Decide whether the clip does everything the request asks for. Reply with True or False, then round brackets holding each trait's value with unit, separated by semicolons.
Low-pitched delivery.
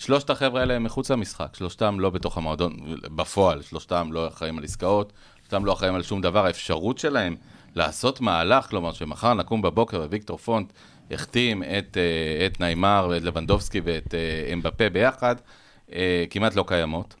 True (95 Hz)